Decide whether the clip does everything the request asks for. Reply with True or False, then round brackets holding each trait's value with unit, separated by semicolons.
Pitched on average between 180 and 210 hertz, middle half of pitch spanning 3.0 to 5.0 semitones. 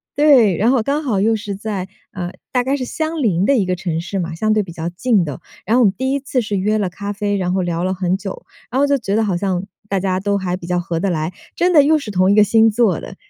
True (200 Hz; 4.6 semitones)